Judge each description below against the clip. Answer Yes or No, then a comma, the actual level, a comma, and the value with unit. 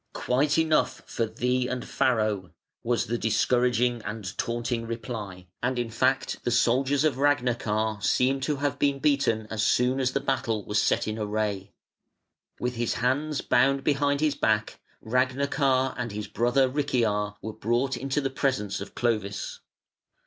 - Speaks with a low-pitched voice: Yes, low, 125 Hz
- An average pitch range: Yes, average, 3.6 semitones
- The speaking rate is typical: Yes, average, 155 wpm